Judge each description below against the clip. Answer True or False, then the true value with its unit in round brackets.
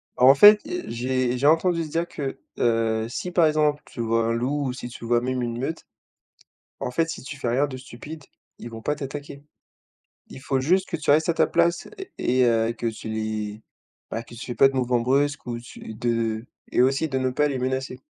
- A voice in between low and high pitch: False (130 Hz)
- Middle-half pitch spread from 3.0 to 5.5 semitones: True (3.9 semitones)